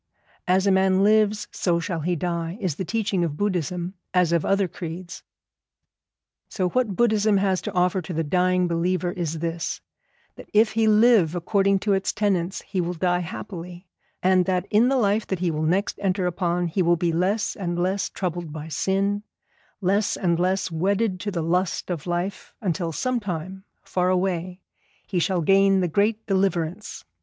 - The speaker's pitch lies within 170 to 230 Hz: Yes, medium, 185 Hz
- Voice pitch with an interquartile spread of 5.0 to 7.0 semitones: No, narrow, 2.4 semitones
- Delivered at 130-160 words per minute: No, average, 175 wpm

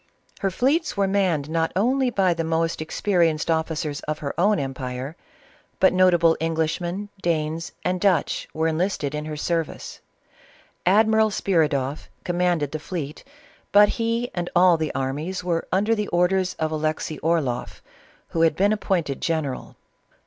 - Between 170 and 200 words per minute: No, average, 150 wpm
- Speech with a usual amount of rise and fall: Yes, average, 3.5 semitones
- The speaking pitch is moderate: Yes, medium, 170 Hz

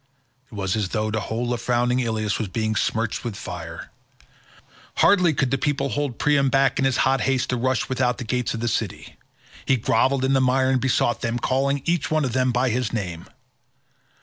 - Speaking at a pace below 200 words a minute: No, fast, 205 wpm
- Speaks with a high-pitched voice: No, low, 125 Hz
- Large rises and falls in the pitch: No, average, 3.1 semitones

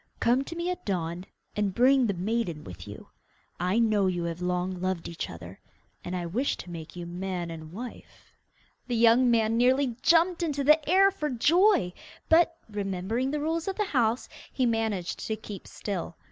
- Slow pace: No, average, 185 wpm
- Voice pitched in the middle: No, high, 220 Hz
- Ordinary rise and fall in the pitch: No, wide, 7.1 semitones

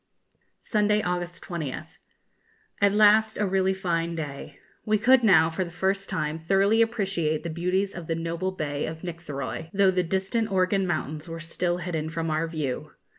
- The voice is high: No, medium, 175 Hz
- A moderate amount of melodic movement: Yes, average, 3.3 semitones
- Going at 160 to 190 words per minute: Yes, average, 170 wpm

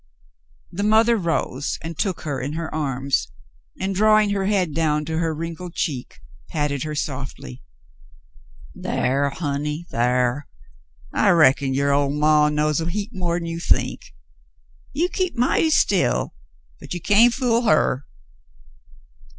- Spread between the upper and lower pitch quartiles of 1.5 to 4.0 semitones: No, average, 5.3 semitones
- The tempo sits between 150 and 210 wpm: No, slow, 135 wpm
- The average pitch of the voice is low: No, medium, 160 Hz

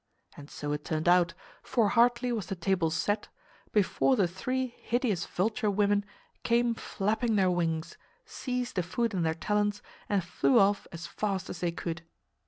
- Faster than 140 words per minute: Yes, average, 170 wpm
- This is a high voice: Yes, high, 200 Hz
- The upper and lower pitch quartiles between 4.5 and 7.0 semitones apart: Yes, average, 4.9 semitones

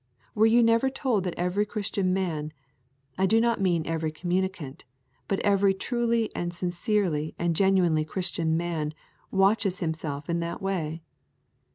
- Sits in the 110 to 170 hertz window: No, medium, 185 Hz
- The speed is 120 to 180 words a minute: Yes, average, 145 wpm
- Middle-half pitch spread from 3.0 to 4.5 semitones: Yes, average, 3.7 semitones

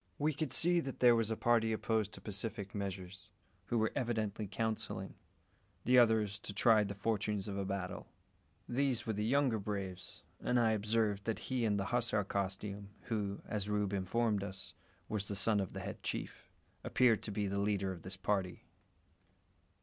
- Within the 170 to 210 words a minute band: Yes, average, 180 wpm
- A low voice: Yes, low, 105 Hz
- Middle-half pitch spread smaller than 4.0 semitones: Yes, narrow, 2.4 semitones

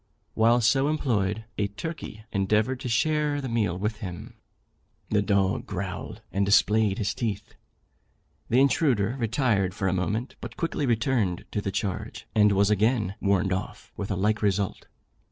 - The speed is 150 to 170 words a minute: Yes, average, 155 wpm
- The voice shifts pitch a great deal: No, average, 3.6 semitones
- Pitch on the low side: Yes, low, 105 Hz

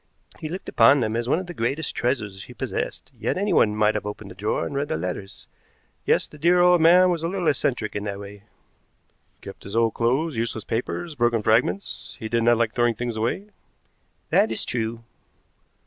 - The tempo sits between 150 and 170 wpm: No, average, 200 wpm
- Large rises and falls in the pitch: Yes, wide, 6.2 semitones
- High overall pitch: No, low, 120 Hz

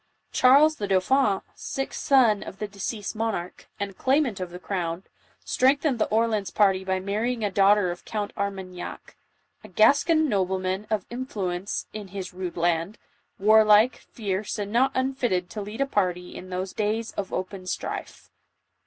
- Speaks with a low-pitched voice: No, high, 205 Hz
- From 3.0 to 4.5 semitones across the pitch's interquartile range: Yes, average, 3.5 semitones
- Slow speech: No, average, 160 wpm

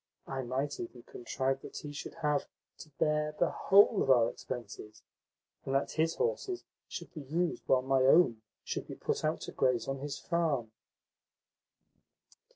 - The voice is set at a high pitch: No, low, 135 Hz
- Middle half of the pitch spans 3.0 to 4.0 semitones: Yes, average, 3.7 semitones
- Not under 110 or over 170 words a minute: Yes, average, 165 wpm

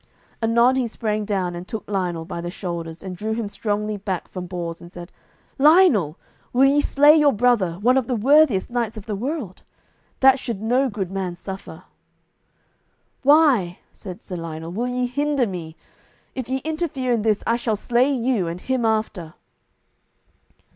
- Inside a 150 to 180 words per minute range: Yes, average, 170 wpm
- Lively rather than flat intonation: Yes, wide, 5.8 semitones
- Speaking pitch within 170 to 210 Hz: No, high, 220 Hz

